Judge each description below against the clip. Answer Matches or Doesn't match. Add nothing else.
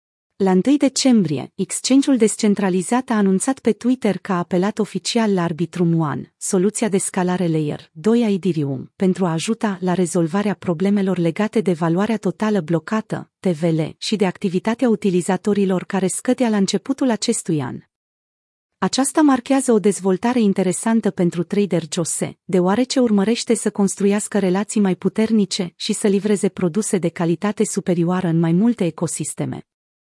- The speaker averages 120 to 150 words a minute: Matches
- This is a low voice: Doesn't match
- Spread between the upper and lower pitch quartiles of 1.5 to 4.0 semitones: Matches